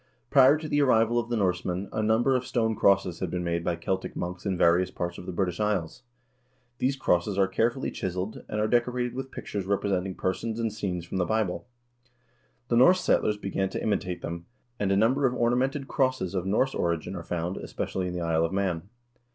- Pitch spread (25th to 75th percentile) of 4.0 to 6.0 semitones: Yes, average, 4.9 semitones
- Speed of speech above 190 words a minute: Yes, fast, 205 wpm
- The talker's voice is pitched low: Yes, low, 100 Hz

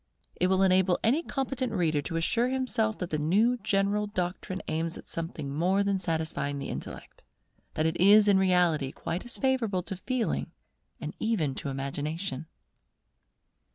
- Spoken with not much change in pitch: No, average, 4.8 semitones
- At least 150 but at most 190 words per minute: Yes, average, 155 wpm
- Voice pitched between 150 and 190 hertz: Yes, medium, 185 Hz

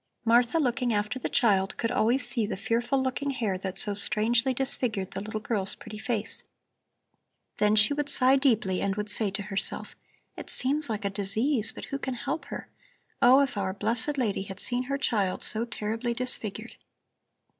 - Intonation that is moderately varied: Yes, average, 3.7 semitones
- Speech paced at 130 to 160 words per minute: No, average, 180 wpm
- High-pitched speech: Yes, high, 230 Hz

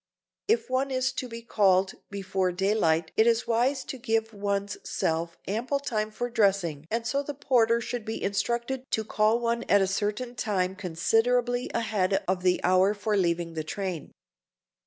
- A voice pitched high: Yes, high, 215 Hz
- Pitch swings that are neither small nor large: Yes, average, 4.0 semitones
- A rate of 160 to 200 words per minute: Yes, average, 170 wpm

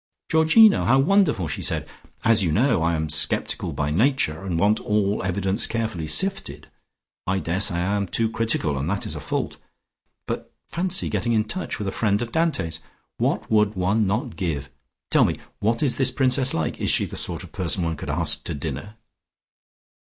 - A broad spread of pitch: Yes, wide, 6.3 semitones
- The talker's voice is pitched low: Yes, low, 100 Hz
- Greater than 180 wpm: Yes, average, 190 wpm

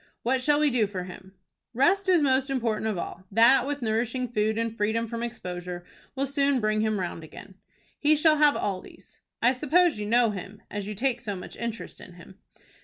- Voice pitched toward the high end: Yes, high, 230 Hz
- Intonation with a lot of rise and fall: No, average, 4.6 semitones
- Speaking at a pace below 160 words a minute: No, fast, 205 wpm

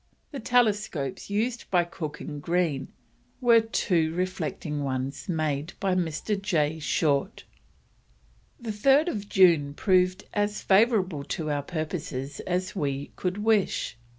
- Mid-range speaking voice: Yes, medium, 180 Hz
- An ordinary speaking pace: No, slow, 125 wpm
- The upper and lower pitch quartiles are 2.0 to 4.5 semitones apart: No, wide, 5.6 semitones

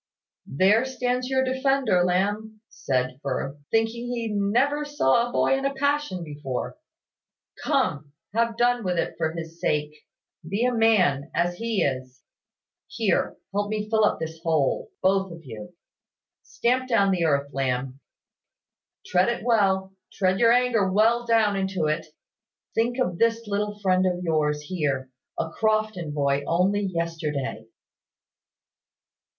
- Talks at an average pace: Yes, average, 145 wpm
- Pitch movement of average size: No, wide, 6.7 semitones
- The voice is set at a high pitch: Yes, high, 195 Hz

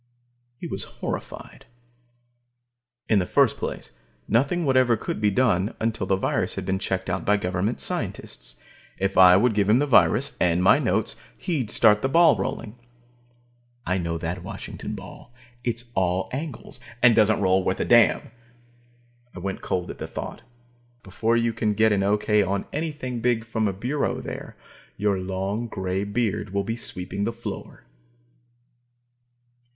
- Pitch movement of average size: Yes, average, 3.9 semitones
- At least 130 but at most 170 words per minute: Yes, average, 160 wpm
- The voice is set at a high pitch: No, low, 105 Hz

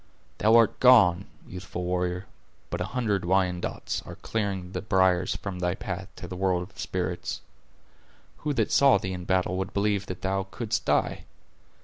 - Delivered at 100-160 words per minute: No, average, 170 wpm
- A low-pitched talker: Yes, very low, 95 Hz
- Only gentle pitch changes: Yes, narrow, 2.0 semitones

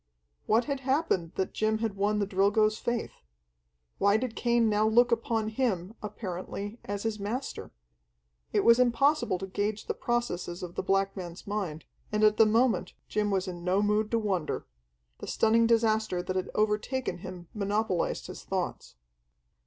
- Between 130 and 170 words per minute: Yes, average, 165 wpm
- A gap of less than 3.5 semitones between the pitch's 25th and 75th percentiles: Yes, average, 2.9 semitones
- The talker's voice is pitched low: No, high, 210 Hz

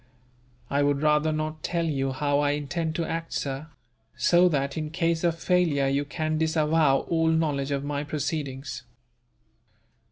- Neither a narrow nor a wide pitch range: No, narrow, 2.3 semitones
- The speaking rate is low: No, average, 155 wpm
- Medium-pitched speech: Yes, medium, 155 Hz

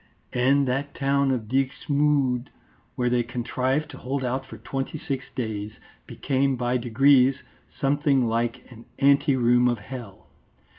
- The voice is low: Yes, low, 130 Hz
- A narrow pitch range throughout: Yes, narrow, 2.2 semitones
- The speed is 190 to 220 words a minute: No, average, 145 wpm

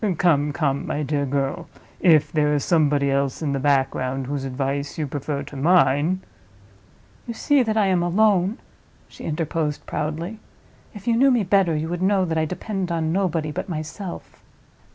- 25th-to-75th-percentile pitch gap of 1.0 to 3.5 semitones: No, average, 4.5 semitones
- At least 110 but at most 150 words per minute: No, average, 175 wpm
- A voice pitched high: No, medium, 155 Hz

